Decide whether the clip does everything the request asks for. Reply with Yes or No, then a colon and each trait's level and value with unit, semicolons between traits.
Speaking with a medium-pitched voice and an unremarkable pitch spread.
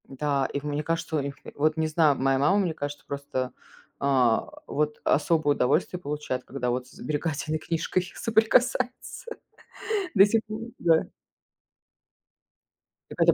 Yes: medium, 150 Hz; average, 3.0 semitones